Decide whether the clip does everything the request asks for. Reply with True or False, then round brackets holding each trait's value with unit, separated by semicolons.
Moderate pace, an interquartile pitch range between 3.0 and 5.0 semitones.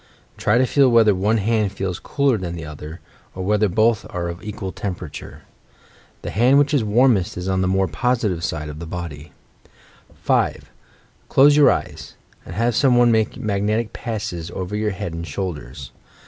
True (180 wpm; 4.7 semitones)